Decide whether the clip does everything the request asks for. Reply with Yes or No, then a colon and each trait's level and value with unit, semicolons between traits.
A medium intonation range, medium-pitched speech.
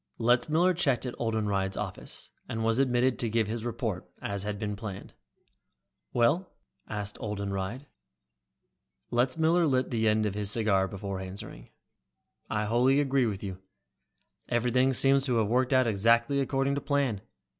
No: average, 4.1 semitones; low, 115 Hz